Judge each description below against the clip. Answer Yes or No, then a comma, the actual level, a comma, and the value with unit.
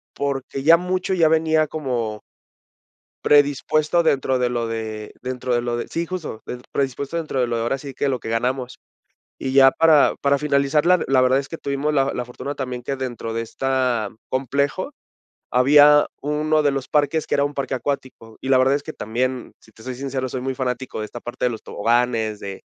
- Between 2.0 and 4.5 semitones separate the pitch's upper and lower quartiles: Yes, average, 2.9 semitones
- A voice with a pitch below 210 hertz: Yes, low, 135 Hz